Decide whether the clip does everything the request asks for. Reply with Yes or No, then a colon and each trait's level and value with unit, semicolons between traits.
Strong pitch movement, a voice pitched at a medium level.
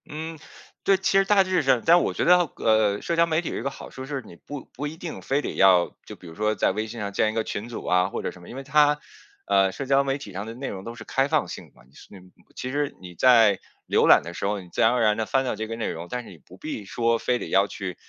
No: wide, 6.0 semitones; low, 115 Hz